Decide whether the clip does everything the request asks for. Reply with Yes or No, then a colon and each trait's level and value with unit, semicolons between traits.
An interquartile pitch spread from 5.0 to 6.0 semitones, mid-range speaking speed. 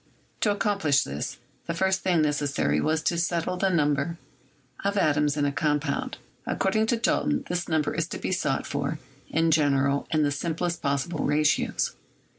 No: average, 3.8 semitones; average, 170 wpm